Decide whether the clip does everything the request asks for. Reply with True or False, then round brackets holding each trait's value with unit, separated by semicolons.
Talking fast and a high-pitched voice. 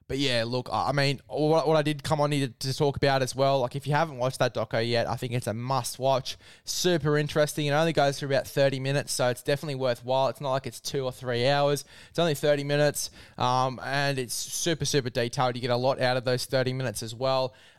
False (245 wpm; 135 Hz)